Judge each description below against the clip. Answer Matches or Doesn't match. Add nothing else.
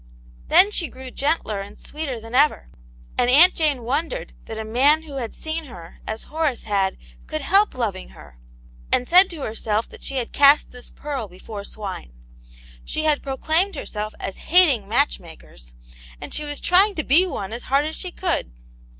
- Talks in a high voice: Matches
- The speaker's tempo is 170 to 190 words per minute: Matches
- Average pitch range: Doesn't match